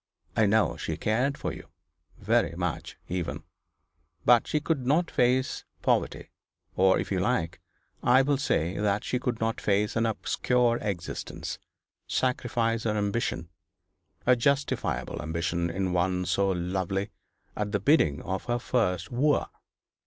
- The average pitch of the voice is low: Yes, low, 105 Hz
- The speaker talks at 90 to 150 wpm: Yes, average, 140 wpm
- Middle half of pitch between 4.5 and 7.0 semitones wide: Yes, average, 5.2 semitones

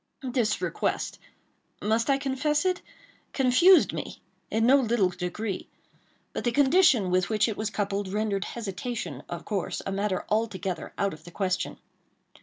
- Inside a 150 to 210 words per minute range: No, average, 140 wpm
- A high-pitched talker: Yes, high, 215 Hz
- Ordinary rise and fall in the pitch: Yes, average, 4.7 semitones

